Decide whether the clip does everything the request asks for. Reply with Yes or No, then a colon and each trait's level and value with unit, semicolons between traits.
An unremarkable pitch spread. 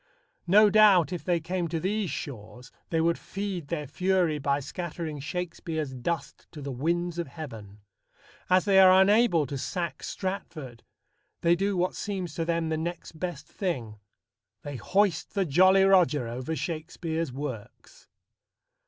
Yes: average, 4.3 semitones